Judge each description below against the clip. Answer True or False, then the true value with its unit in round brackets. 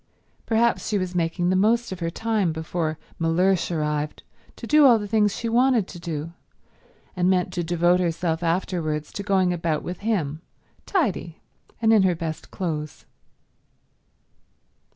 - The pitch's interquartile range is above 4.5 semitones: False (4.0 semitones)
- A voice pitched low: False (180 Hz)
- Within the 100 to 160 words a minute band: True (155 wpm)